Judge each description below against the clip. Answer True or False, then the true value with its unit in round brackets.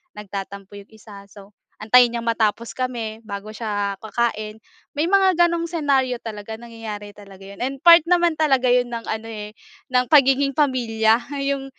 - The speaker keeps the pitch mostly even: False (4.2 semitones)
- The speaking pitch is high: True (230 Hz)